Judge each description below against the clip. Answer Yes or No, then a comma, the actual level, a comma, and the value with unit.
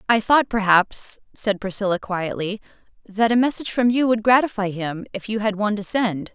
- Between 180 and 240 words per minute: Yes, average, 190 wpm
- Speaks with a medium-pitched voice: No, high, 210 Hz